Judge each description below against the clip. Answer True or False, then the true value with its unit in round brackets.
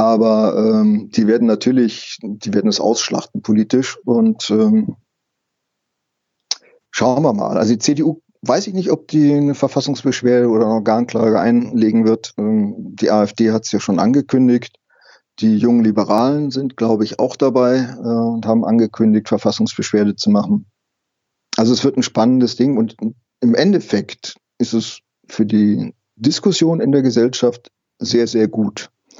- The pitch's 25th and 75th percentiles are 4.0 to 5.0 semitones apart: True (4.4 semitones)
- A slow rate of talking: False (150 wpm)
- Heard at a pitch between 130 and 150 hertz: False (120 Hz)